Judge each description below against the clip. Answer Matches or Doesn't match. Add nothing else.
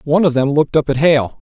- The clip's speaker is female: Doesn't match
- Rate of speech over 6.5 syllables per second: Matches